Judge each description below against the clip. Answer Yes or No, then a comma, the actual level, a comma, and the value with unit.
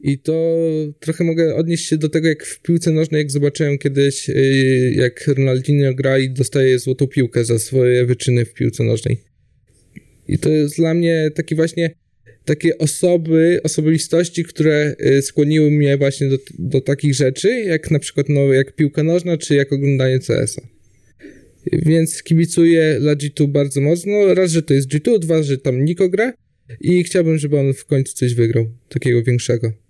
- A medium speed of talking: No, fast, 170 wpm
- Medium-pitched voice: Yes, medium, 145 Hz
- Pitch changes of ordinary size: Yes, average, 3.5 semitones